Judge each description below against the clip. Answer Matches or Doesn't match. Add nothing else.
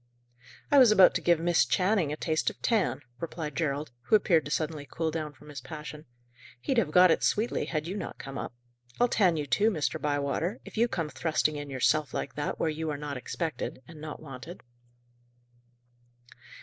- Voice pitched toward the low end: Doesn't match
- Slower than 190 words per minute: Doesn't match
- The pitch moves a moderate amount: Matches